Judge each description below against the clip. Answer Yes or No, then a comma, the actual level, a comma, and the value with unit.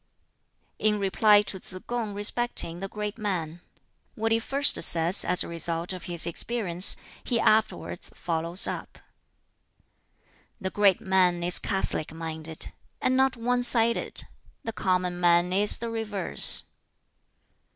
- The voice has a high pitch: Yes, high, 195 Hz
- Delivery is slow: Yes, slow, 130 wpm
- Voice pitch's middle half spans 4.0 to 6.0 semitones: Yes, average, 4.3 semitones